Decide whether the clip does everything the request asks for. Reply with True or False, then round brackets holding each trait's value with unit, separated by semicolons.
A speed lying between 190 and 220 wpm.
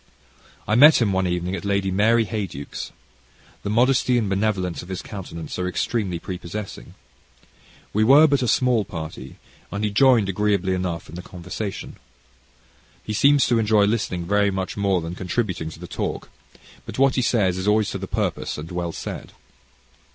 False (175 wpm)